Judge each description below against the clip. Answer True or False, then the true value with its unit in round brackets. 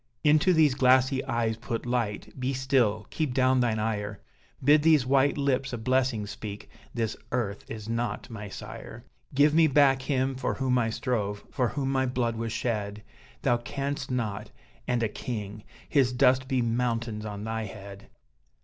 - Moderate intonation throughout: True (3.2 semitones)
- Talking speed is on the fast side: False (165 wpm)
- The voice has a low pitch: True (125 Hz)